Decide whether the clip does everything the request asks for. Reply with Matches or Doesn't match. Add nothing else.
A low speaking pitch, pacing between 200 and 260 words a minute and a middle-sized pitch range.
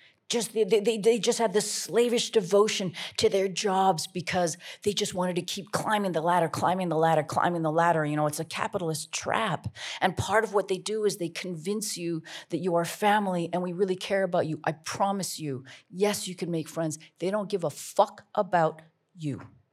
Doesn't match